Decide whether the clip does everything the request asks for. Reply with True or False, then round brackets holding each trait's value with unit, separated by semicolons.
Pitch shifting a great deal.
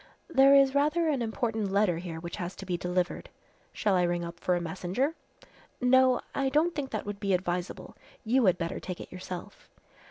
True (6.8 semitones)